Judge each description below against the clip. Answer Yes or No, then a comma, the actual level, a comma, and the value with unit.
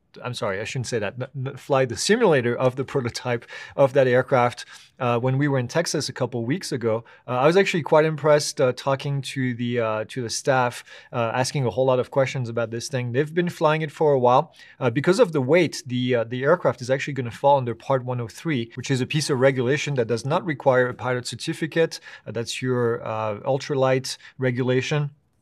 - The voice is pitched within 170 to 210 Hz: No, low, 130 Hz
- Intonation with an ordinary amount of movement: Yes, average, 3.0 semitones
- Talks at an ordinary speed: No, fast, 215 wpm